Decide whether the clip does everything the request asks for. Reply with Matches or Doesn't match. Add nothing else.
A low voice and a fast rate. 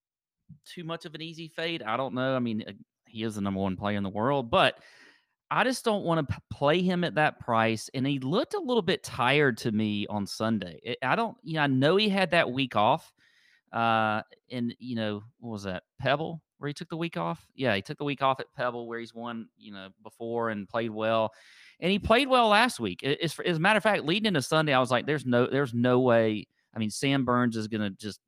Matches